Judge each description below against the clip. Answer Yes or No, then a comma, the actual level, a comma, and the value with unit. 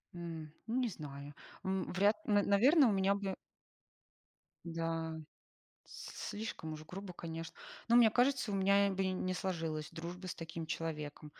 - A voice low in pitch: No, medium, 185 Hz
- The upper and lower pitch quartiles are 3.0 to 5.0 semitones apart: Yes, average, 3.8 semitones